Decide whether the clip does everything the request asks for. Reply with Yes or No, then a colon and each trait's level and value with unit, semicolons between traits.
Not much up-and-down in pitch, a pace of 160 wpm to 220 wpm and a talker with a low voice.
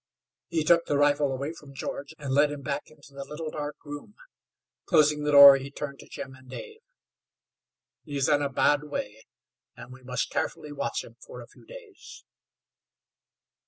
No: narrow, 1.6 semitones; average, 180 wpm; medium, 145 Hz